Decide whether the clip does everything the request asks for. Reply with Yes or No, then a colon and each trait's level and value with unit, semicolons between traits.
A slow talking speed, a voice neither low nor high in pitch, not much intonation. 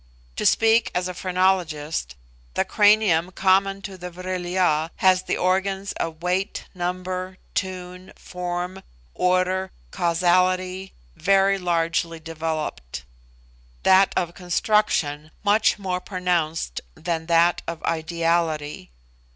Yes: slow, 110 wpm; medium, 180 Hz; narrow, 2.1 semitones